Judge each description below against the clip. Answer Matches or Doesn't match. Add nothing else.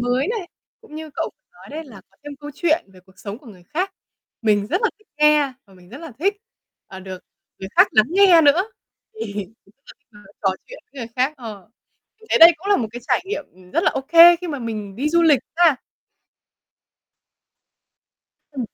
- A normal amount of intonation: Doesn't match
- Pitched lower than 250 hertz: Doesn't match